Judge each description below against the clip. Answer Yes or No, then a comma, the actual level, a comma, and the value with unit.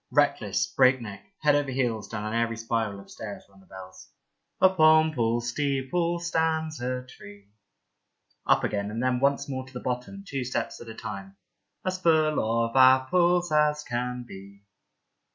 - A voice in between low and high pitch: No, low, 125 Hz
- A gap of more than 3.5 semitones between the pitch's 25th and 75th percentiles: Yes, wide, 5.4 semitones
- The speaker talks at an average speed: Yes, average, 170 wpm